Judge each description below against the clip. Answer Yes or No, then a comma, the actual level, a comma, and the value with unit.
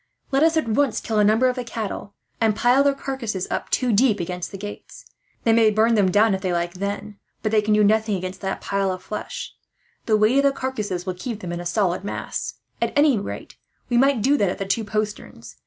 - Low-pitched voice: No, high, 215 Hz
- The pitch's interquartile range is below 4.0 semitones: Yes, average, 3.6 semitones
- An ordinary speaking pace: No, fast, 235 wpm